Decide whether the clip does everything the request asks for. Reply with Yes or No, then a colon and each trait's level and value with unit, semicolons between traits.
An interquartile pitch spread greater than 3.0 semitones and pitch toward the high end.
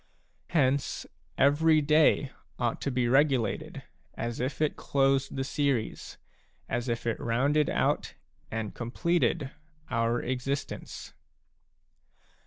No: average, 3.4 semitones; low, 135 Hz